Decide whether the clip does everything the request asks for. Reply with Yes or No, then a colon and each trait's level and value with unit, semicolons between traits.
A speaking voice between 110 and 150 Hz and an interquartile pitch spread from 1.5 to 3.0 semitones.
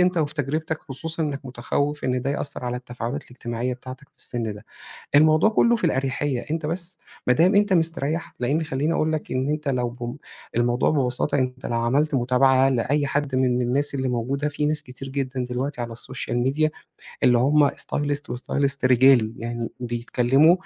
No: low, 135 Hz; average, 3.4 semitones